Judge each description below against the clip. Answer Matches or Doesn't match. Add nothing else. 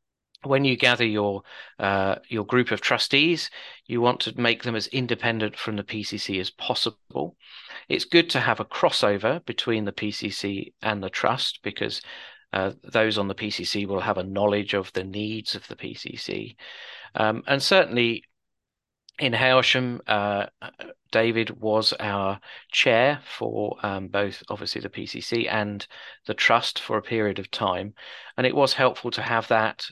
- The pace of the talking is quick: Doesn't match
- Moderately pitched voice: Doesn't match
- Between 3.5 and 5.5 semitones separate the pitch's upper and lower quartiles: Doesn't match